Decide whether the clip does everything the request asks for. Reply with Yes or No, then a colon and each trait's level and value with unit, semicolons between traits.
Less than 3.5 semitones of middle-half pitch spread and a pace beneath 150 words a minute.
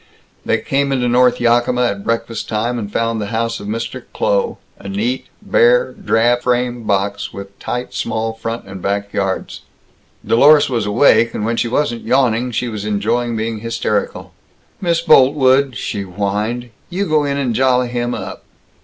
No: average, 3.0 semitones; average, 165 wpm